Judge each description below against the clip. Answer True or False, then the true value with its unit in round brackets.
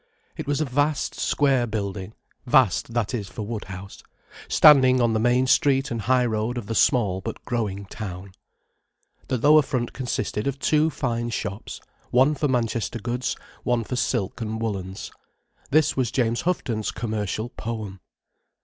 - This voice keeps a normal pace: True (150 wpm)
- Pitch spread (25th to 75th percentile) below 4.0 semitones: True (3.4 semitones)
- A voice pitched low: True (120 Hz)